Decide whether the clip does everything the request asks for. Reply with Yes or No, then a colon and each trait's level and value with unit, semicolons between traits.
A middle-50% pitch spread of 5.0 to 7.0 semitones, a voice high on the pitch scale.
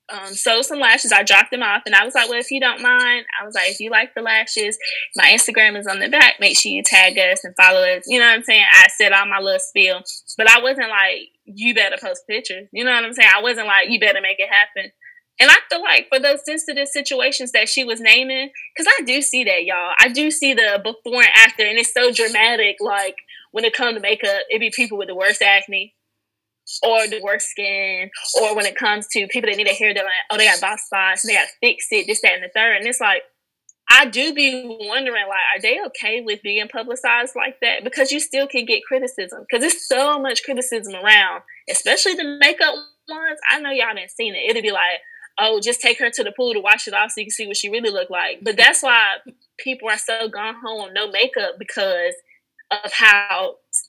Yes: average, 5.3 semitones; high, 230 Hz